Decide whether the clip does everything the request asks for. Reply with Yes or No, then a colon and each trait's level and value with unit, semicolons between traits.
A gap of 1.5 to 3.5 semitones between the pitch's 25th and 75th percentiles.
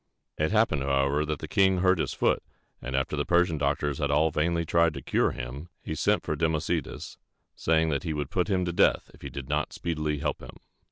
Yes: average, 2.8 semitones